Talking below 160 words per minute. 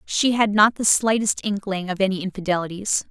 No: average, 175 wpm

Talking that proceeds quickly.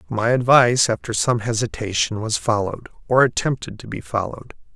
No: average, 150 wpm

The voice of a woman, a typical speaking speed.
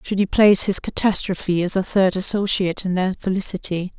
Yes: female; average, 180 wpm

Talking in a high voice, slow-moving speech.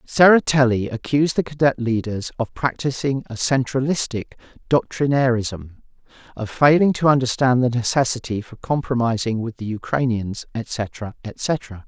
No: low, 125 Hz; slow, 115 wpm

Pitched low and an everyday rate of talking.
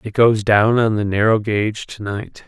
No: low, 105 Hz; fast, 220 wpm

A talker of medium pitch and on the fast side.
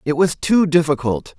No: medium, 160 Hz; average, 175 wpm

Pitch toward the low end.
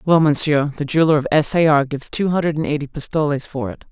No: medium, 150 Hz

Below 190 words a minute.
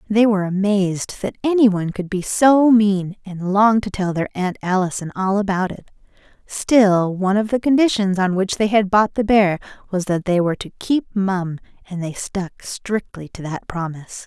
No: average, 195 wpm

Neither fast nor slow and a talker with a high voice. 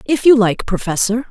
Yes: average, 185 wpm; high, 230 Hz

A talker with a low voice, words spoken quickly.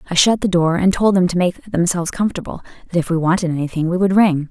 No: medium, 175 Hz; fast, 255 wpm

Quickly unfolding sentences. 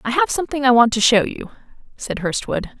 Yes: fast, 215 wpm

